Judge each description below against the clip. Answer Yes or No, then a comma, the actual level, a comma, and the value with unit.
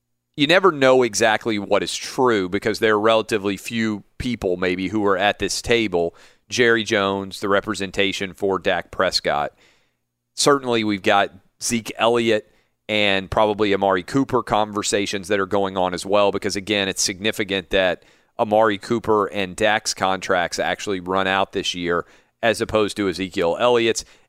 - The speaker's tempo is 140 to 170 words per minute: Yes, average, 155 wpm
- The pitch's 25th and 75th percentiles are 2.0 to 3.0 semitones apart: Yes, narrow, 2.6 semitones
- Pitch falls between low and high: No, low, 105 Hz